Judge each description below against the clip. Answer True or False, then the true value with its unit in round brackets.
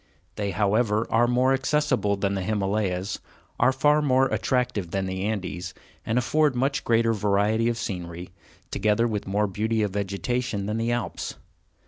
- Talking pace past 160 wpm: False (155 wpm)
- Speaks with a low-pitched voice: True (110 Hz)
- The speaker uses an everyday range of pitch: True (3.6 semitones)